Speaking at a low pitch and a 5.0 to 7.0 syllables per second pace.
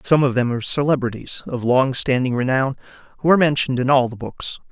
Yes: low, 130 Hz; 6.2 syllables/s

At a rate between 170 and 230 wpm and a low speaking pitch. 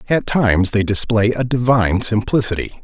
No: average, 150 wpm; low, 110 Hz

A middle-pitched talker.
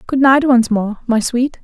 No: high, 245 Hz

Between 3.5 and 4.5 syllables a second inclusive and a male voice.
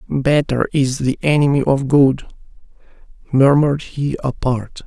Yes: 4.4 syllables/s; male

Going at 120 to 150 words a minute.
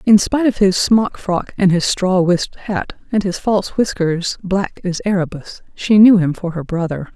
No: average, 200 wpm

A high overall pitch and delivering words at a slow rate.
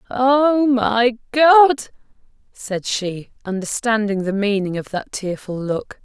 Yes: high, 225 Hz; slow, 120 wpm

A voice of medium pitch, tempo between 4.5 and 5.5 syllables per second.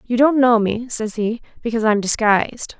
No: high, 230 Hz; 5.3 syllables/s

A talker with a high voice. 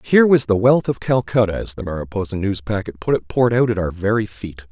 No: low, 105 Hz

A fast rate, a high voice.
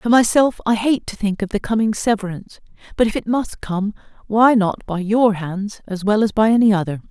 Yes: fast, 220 wpm; high, 210 Hz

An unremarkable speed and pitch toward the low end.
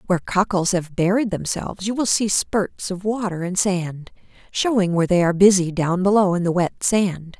No: average, 195 wpm; high, 190 Hz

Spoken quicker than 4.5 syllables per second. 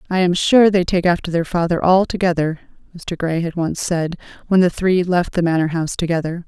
Yes: 5.5 syllables/s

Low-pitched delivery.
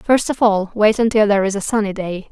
No: high, 210 Hz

